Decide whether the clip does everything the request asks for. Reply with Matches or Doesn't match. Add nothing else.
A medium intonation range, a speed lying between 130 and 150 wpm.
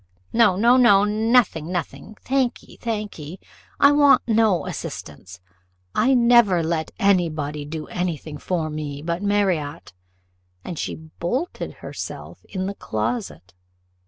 Doesn't match